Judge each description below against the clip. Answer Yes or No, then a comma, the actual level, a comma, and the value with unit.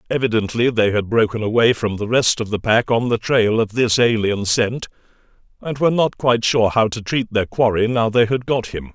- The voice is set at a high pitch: No, low, 115 Hz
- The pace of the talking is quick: Yes, fast, 220 wpm